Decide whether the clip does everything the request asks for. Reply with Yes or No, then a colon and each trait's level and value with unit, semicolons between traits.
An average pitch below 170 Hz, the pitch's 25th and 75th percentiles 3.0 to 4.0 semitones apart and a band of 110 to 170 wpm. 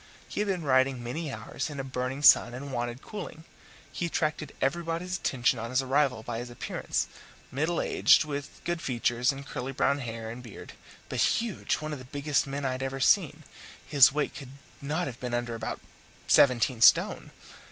No: low, 135 Hz; average, 3.6 semitones; average, 185 wpm